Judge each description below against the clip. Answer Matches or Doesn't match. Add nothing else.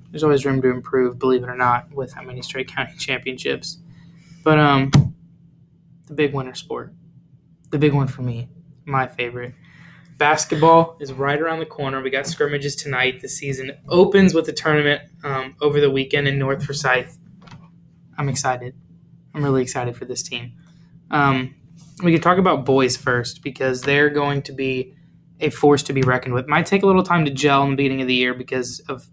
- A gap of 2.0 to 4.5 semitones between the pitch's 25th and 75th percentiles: Matches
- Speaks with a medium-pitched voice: Matches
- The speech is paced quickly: Doesn't match